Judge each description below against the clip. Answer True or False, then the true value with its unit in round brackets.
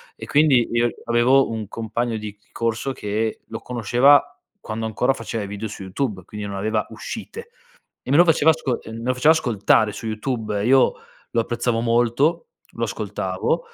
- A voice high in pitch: False (115 Hz)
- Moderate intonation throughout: True (3.4 semitones)